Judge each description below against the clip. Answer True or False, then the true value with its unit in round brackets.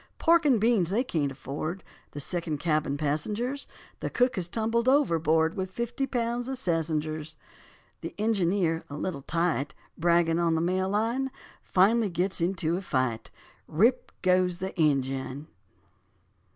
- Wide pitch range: True (6.1 semitones)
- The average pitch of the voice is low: False (175 Hz)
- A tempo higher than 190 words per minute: False (140 wpm)